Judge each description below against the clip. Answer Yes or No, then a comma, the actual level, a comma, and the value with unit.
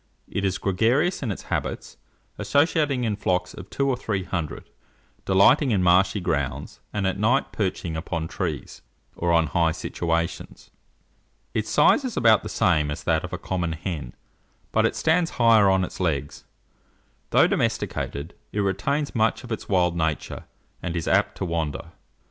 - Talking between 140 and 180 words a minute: Yes, average, 165 wpm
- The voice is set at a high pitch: No, very low, 95 Hz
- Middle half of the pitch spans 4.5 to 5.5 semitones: Yes, average, 5.2 semitones